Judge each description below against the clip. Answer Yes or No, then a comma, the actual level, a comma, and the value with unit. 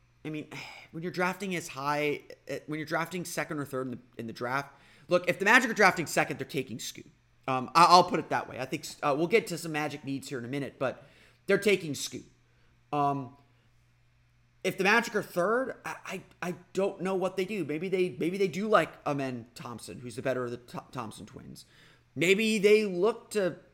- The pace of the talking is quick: Yes, fast, 215 wpm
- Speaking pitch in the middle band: Yes, medium, 150 Hz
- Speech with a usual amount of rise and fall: No, wide, 6.0 semitones